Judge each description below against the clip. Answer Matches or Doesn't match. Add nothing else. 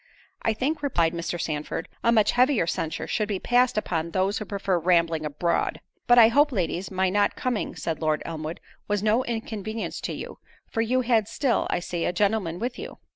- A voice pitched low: Doesn't match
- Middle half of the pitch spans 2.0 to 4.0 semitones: Doesn't match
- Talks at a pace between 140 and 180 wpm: Doesn't match